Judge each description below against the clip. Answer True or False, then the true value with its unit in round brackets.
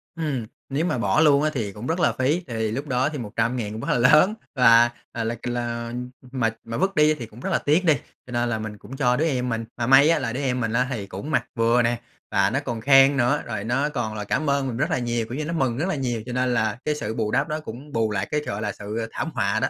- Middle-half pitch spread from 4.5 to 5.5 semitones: False (3.8 semitones)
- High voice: False (125 Hz)